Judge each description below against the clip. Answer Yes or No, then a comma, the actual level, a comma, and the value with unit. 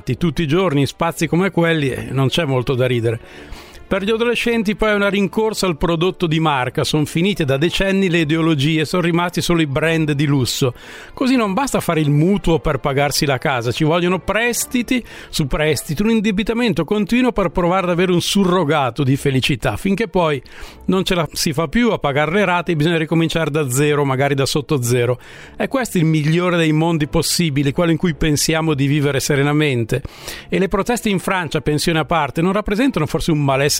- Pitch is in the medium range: Yes, medium, 165 Hz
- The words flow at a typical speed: No, fast, 195 wpm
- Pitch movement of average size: Yes, average, 4.5 semitones